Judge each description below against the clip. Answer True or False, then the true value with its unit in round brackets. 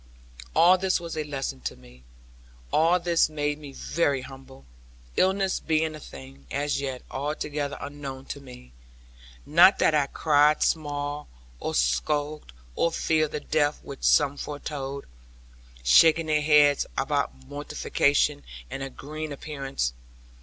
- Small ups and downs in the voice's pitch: True (2.3 semitones)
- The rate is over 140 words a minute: False (135 wpm)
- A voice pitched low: False (145 Hz)